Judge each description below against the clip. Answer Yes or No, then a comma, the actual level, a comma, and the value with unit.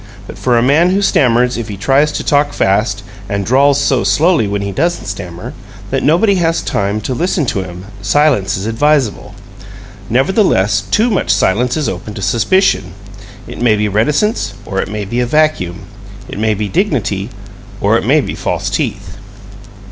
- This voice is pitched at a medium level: No, low, 120 Hz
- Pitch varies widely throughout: Yes, wide, 6.9 semitones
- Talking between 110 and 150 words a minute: No, average, 180 wpm